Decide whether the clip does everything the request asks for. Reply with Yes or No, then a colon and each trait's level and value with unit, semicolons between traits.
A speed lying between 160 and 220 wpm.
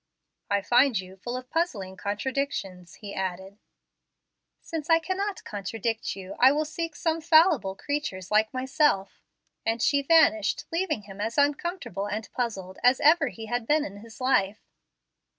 No: average, 150 wpm